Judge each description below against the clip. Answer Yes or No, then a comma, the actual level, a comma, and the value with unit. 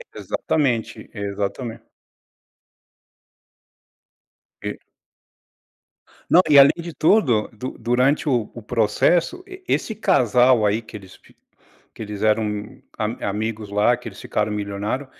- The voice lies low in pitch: Yes, low, 115 Hz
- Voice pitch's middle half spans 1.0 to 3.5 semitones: No, average, 4.2 semitones